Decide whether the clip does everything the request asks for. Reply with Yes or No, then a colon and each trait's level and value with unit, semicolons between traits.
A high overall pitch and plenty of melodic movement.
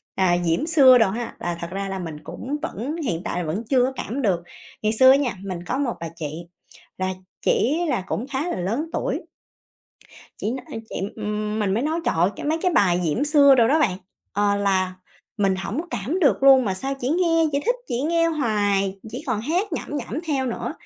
Yes: high, 230 Hz; wide, 6.6 semitones